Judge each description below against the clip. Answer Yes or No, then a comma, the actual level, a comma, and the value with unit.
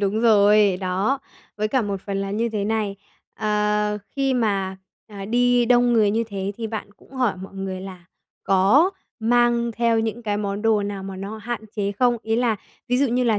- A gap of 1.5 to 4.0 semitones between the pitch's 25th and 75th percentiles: Yes, average, 3.0 semitones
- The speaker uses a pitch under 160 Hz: No, high, 215 Hz